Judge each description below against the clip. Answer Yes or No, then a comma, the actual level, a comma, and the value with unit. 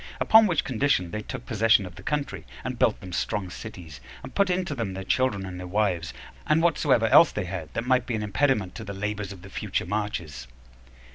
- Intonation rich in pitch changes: Yes, wide, 5.7 semitones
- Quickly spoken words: Yes, fast, 215 wpm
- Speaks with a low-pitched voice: Yes, low, 105 Hz